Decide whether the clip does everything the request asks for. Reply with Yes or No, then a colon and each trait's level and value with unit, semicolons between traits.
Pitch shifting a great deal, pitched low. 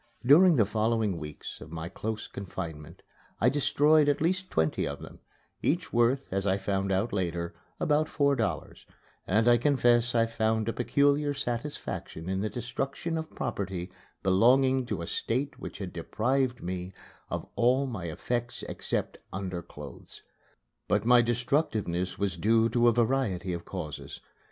Yes: wide, 5.8 semitones; low, 115 Hz